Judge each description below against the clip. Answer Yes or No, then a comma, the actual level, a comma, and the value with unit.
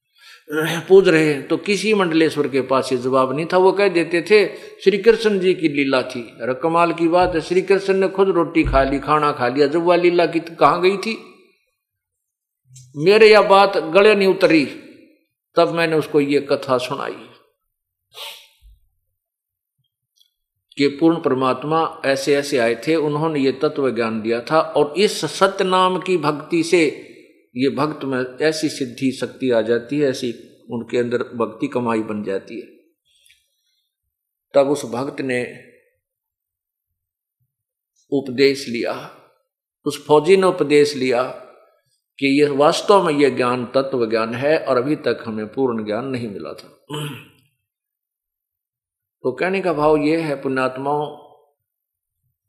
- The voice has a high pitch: No, medium, 145 Hz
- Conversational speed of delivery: Yes, average, 145 wpm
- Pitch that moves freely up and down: Yes, wide, 5.9 semitones